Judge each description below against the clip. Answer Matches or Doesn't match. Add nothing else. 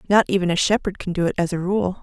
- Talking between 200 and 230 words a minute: Doesn't match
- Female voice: Matches